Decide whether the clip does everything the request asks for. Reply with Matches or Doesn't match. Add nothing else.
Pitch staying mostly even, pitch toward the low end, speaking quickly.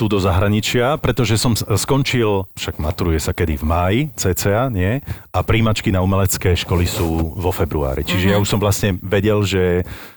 Doesn't match